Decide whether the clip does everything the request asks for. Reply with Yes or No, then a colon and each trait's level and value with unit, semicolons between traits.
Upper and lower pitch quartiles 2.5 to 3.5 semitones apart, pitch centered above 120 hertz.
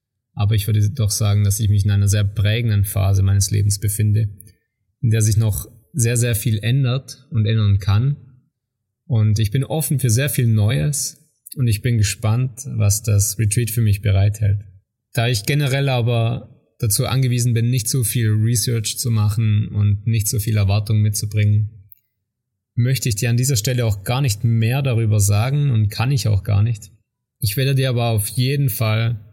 No: average, 2.8 semitones; low, 115 Hz